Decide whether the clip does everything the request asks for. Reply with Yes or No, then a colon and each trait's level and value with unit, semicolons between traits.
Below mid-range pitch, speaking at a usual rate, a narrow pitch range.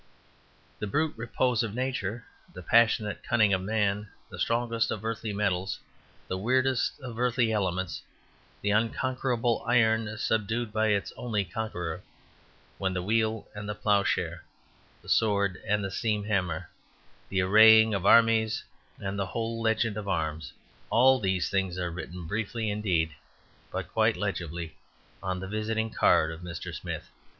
No: low, 105 Hz; average, 145 wpm; average, 3.1 semitones